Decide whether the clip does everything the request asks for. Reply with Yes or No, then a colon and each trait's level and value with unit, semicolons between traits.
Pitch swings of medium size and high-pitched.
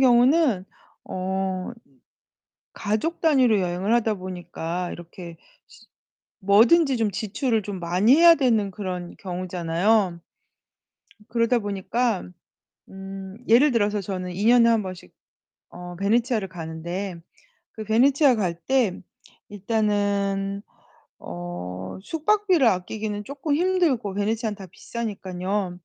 Yes: average, 4.4 semitones; high, 205 Hz